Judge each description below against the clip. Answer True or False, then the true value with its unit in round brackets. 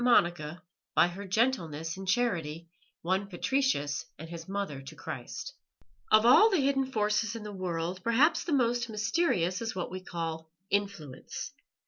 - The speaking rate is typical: True (150 wpm)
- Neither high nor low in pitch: False (195 Hz)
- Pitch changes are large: True (5.9 semitones)